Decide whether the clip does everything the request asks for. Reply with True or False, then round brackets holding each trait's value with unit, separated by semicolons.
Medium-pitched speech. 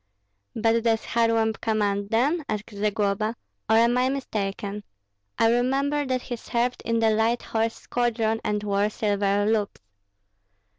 False (225 Hz)